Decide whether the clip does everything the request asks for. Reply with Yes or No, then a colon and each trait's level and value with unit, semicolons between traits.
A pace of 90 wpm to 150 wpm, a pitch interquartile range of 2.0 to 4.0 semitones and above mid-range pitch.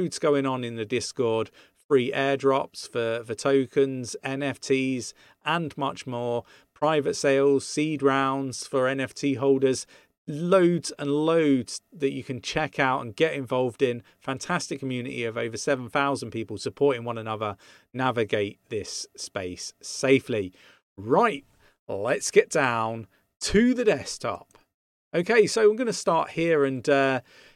No: slow, 135 wpm; average, 3.4 semitones; low, 135 Hz